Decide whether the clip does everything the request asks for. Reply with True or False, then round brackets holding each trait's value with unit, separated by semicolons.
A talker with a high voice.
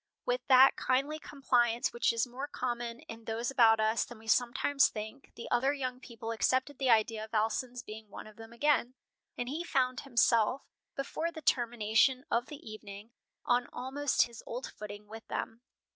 True (240 Hz)